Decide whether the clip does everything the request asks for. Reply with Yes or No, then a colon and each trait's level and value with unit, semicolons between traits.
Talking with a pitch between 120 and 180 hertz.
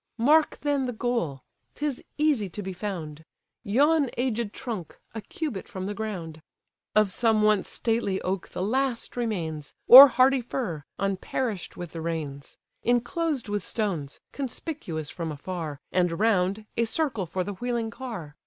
No: high, 210 Hz